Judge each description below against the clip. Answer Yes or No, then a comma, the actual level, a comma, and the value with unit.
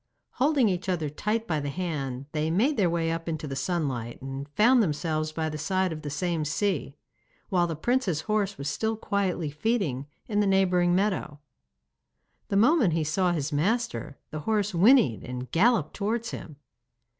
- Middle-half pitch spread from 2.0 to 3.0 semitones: No, wide, 5.5 semitones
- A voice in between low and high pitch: Yes, medium, 175 Hz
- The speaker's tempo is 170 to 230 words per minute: Yes, average, 175 wpm